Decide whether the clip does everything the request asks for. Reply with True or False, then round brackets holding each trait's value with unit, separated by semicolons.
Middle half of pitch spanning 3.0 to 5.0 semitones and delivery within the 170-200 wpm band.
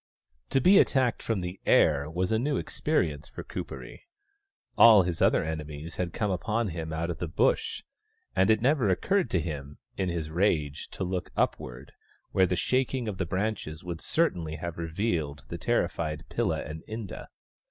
False (5.6 semitones; 175 wpm)